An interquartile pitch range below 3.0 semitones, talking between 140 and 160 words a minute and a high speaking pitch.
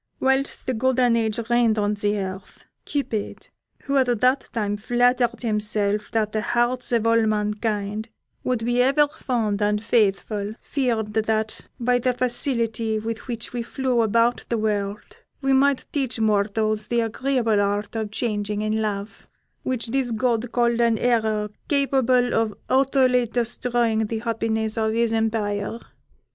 Yes: narrow, 2.6 semitones; average, 150 wpm; high, 225 Hz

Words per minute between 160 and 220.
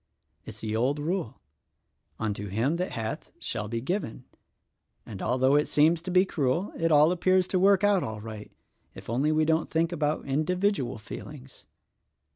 Yes: average, 170 wpm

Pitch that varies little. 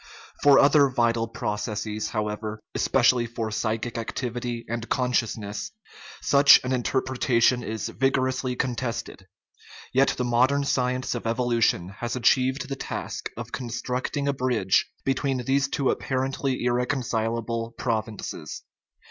Yes: narrow, 2.3 semitones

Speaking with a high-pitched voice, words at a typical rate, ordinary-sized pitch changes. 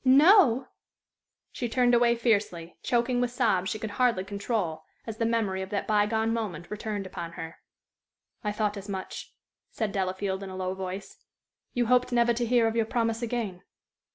Yes: high, 220 Hz; average, 180 wpm; average, 3.8 semitones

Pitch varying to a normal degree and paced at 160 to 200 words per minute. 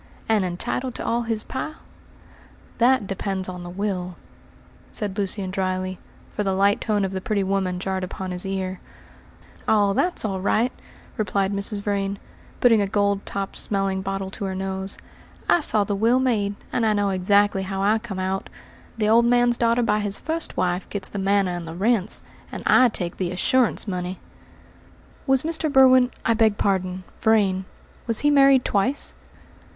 Yes: average, 3.1 semitones; average, 170 wpm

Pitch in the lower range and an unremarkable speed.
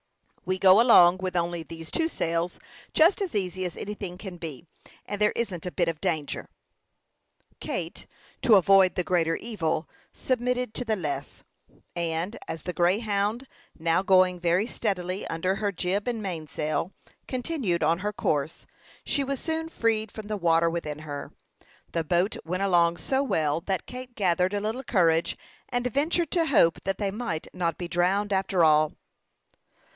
No: medium, 185 Hz; average, 165 wpm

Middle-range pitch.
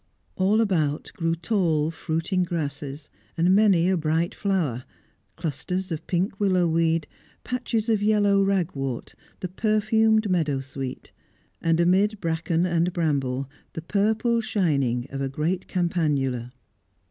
Yes: medium, 170 Hz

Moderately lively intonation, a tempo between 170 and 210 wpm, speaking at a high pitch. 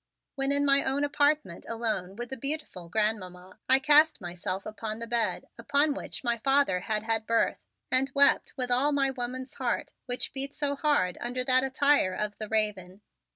Yes: average, 4.6 semitones; average, 180 wpm; high, 245 Hz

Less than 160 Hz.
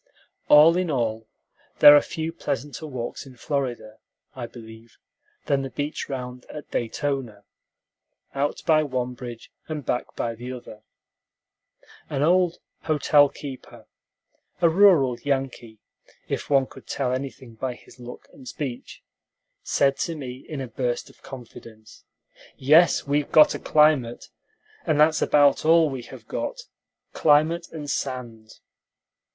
Yes: low, 135 Hz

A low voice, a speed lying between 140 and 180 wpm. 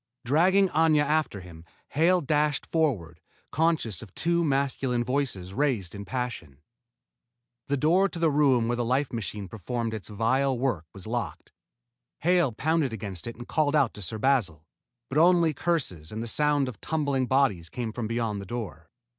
Yes: low, 125 Hz; average, 170 wpm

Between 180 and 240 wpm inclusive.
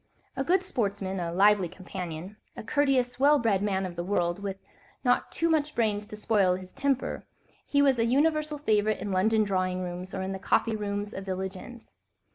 Yes: average, 195 wpm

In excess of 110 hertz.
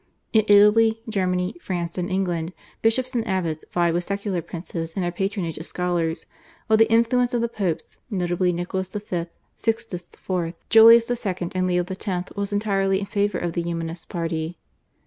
Yes: medium, 185 Hz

